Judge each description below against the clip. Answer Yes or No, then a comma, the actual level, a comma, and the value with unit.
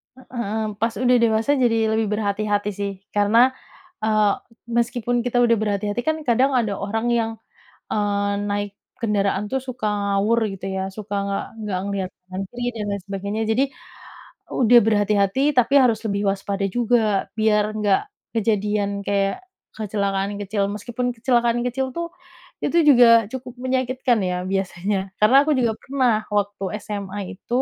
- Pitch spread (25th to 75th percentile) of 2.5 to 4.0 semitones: Yes, average, 3.0 semitones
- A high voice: Yes, high, 215 Hz